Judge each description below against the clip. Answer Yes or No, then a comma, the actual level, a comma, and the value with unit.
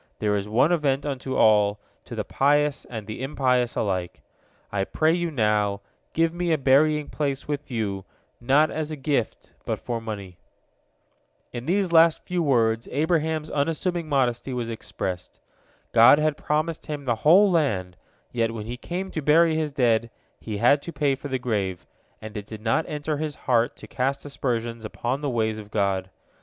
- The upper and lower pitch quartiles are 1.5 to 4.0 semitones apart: No, wide, 5.6 semitones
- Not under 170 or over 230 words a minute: Yes, average, 175 wpm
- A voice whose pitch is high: No, low, 135 Hz